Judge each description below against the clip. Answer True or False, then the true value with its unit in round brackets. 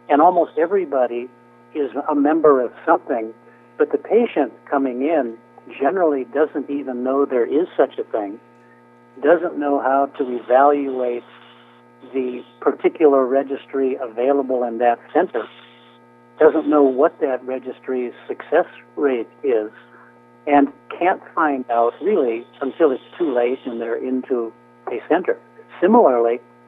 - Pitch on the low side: True (130 Hz)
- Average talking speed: False (130 wpm)